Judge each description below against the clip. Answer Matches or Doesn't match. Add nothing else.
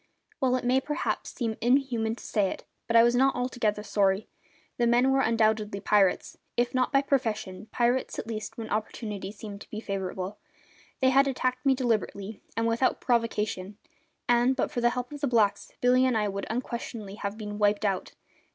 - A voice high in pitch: Matches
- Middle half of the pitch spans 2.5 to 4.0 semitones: Matches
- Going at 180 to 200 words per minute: Matches